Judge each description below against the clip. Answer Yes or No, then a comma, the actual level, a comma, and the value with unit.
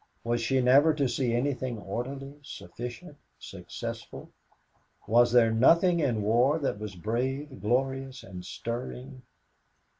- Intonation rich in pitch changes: No, average, 2.8 semitones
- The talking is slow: Yes, slow, 120 wpm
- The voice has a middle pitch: No, low, 125 Hz